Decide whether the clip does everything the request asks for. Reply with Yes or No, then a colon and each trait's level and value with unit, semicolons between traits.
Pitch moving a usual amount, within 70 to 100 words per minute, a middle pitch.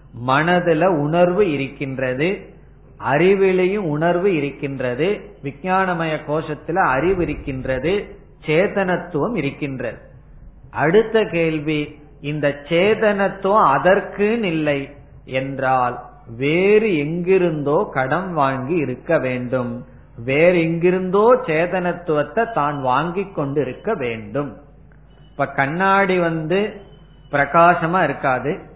Yes: average, 4.8 semitones; average, 80 wpm; medium, 155 Hz